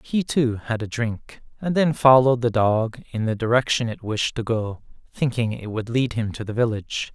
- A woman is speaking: No, male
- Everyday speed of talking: No, fast, 210 wpm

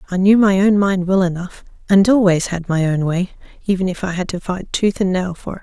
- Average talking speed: No, fast, 255 wpm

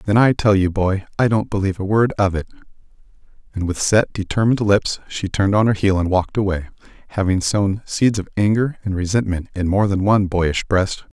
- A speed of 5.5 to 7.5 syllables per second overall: Yes, 5.7 syllables/s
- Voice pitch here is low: Yes, low, 100 Hz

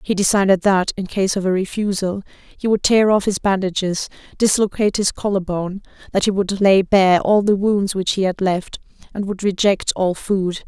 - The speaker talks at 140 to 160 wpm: No, average, 195 wpm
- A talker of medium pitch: No, high, 195 Hz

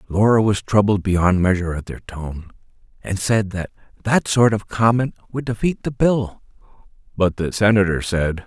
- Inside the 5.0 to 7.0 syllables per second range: No, 4.7 syllables/s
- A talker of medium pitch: No, low, 100 Hz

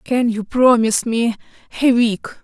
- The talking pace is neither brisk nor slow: Yes, average, 150 wpm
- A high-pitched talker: Yes, high, 235 Hz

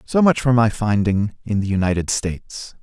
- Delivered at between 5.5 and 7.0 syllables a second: No, 5.0 syllables/s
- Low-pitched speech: Yes, low, 110 Hz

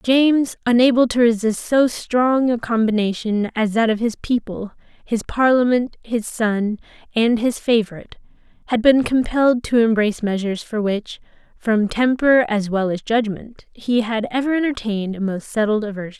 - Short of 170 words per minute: Yes, average, 155 wpm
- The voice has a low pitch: No, high, 230 Hz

